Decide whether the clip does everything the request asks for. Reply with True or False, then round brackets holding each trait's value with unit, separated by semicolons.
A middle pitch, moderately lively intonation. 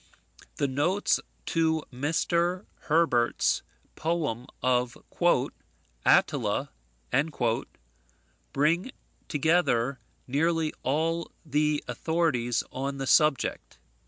True (150 Hz; 3.9 semitones)